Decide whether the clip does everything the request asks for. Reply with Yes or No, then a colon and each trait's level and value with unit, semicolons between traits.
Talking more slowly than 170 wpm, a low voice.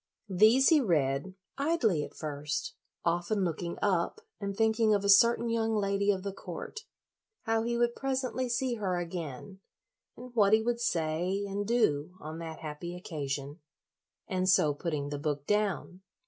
No: average, 160 wpm; high, 195 Hz